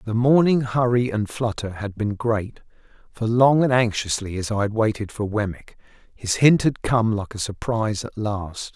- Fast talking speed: No, average, 185 wpm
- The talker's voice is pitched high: No, low, 110 Hz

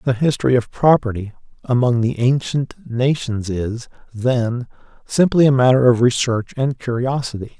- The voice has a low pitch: Yes, low, 125 Hz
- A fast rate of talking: No, slow, 135 wpm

